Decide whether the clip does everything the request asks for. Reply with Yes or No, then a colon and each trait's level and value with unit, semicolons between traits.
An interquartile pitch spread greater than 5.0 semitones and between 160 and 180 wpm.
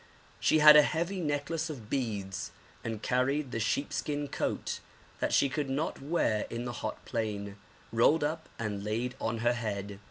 Yes: wide, 5.4 semitones; average, 170 wpm